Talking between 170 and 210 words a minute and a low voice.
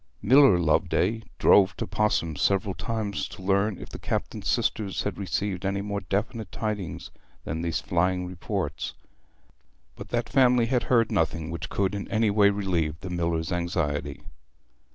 No: average, 155 wpm; very low, 95 Hz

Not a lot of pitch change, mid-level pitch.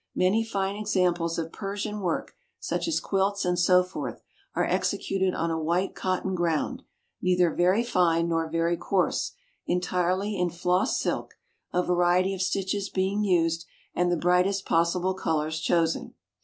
Yes: narrow, 2.2 semitones; medium, 180 Hz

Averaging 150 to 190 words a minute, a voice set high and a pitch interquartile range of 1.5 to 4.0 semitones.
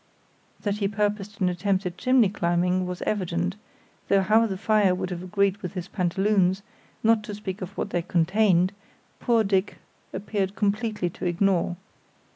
Yes: average, 160 wpm; high, 195 Hz; narrow, 2.5 semitones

